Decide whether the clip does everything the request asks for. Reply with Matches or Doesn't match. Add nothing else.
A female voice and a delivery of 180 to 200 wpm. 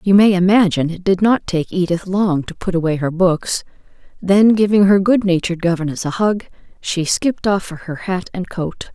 Matches